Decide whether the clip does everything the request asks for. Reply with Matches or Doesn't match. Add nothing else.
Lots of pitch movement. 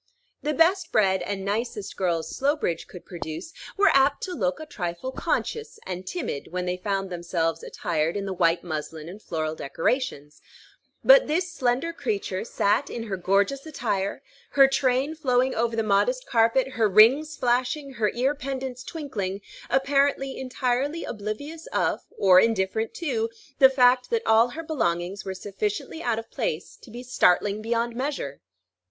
Matches